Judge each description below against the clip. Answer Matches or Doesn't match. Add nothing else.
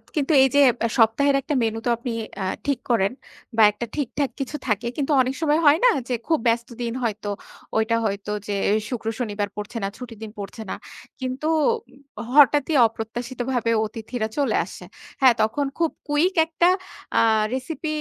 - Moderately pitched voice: Doesn't match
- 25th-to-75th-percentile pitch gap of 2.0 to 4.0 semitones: Doesn't match